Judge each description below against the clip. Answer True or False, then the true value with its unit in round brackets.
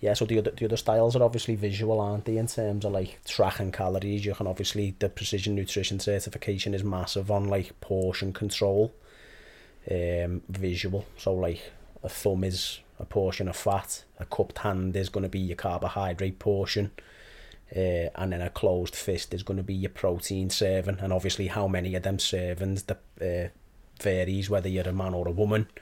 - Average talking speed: True (190 wpm)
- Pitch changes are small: True (1.8 semitones)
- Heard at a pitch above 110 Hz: False (95 Hz)